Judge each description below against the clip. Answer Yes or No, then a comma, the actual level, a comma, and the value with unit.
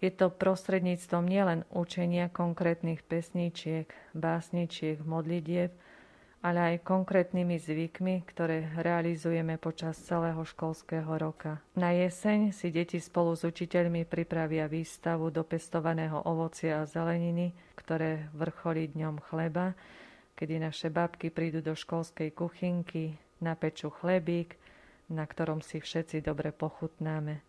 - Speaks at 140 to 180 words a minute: No, average, 115 wpm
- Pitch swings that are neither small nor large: No, narrow, 1.5 semitones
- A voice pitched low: No, medium, 165 Hz